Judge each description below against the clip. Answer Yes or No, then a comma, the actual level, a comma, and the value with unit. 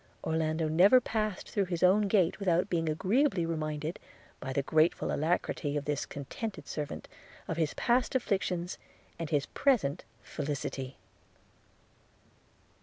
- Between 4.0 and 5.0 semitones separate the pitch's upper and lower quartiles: Yes, average, 4.7 semitones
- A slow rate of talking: Yes, slow, 130 wpm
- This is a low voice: No, medium, 165 Hz